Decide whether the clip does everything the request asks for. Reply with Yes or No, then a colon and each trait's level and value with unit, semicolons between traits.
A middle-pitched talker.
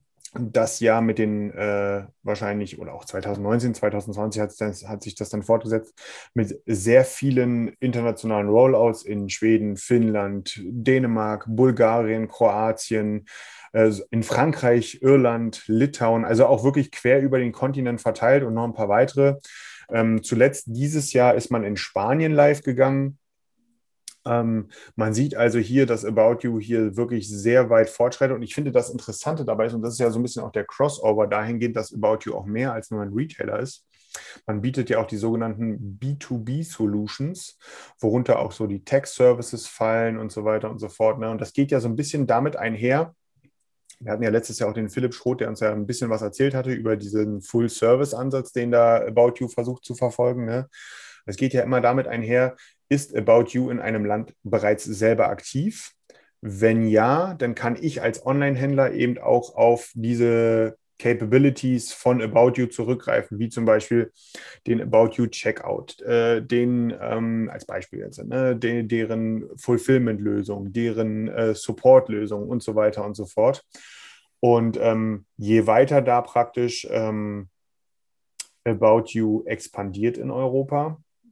No: low, 115 Hz